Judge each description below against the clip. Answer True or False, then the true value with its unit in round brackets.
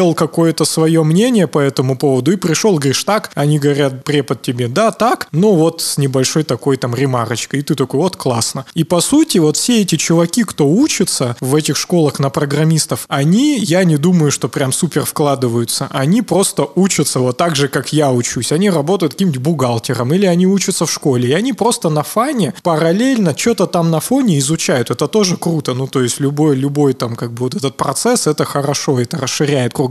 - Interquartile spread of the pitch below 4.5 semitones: False (4.8 semitones)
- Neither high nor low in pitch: True (155 Hz)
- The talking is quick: True (195 wpm)